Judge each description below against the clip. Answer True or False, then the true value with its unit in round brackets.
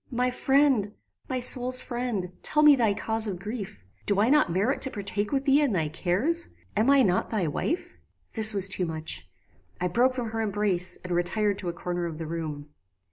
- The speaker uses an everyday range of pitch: False (6.0 semitones)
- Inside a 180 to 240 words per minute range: True (200 wpm)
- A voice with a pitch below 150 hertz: False (210 Hz)